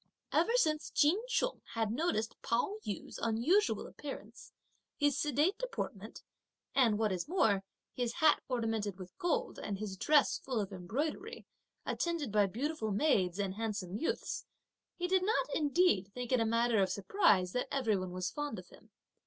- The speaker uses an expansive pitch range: Yes, wide, 7.3 semitones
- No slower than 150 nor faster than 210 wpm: Yes, average, 160 wpm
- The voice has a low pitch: No, high, 235 Hz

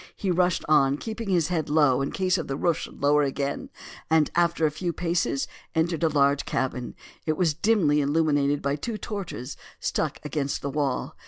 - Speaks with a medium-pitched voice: Yes, medium, 155 Hz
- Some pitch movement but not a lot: Yes, average, 3.5 semitones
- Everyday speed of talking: Yes, average, 180 wpm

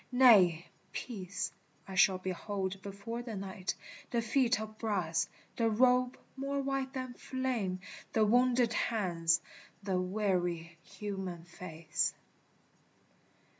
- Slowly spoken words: Yes, slow, 110 wpm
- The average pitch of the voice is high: Yes, high, 205 Hz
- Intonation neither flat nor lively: Yes, average, 4.9 semitones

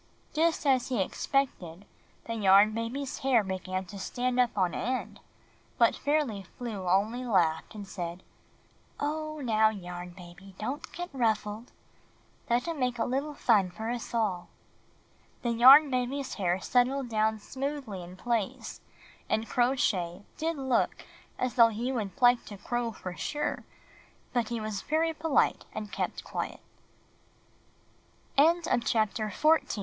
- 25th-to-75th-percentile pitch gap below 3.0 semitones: No, average, 5.0 semitones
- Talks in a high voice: Yes, high, 230 Hz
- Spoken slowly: Yes, slow, 130 wpm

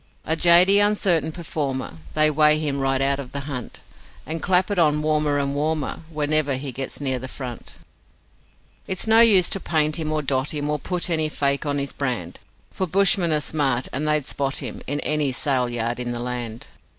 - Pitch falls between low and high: Yes, medium, 150 Hz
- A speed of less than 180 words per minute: No, average, 200 wpm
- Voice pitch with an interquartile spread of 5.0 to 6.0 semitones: No, average, 2.9 semitones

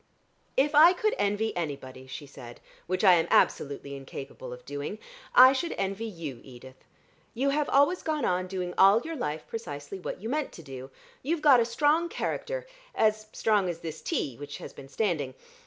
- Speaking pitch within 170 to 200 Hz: Yes, high, 190 Hz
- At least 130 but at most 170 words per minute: No, average, 185 wpm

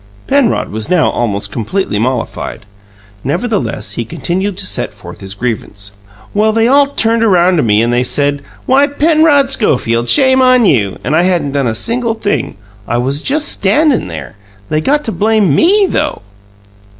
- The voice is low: No, medium, 185 Hz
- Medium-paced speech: Yes, average, 170 wpm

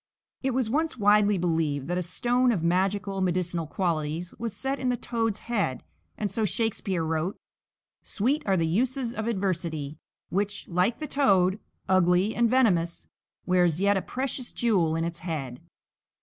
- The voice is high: Yes, high, 195 Hz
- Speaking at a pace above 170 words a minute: No, average, 160 wpm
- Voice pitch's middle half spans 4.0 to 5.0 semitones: No, wide, 5.4 semitones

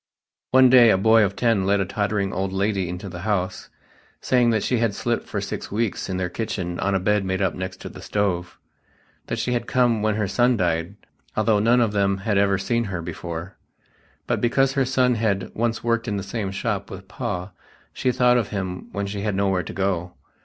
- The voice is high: No, low, 100 Hz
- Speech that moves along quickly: Yes, fast, 215 wpm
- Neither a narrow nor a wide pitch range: Yes, average, 3.5 semitones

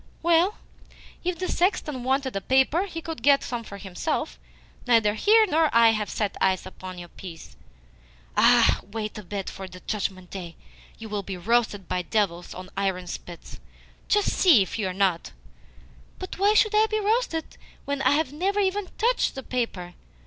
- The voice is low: No, high, 230 Hz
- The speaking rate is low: No, average, 180 wpm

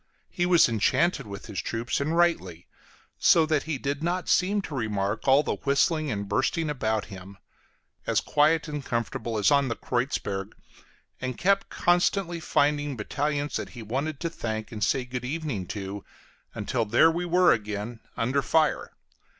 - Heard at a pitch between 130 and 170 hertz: Yes, low, 135 Hz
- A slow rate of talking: No, average, 165 wpm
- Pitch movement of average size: No, wide, 6.4 semitones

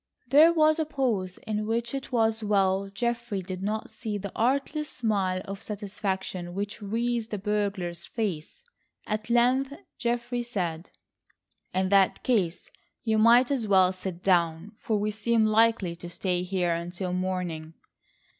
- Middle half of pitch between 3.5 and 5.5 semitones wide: Yes, average, 4.1 semitones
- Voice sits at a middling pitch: No, high, 210 Hz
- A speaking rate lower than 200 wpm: Yes, average, 145 wpm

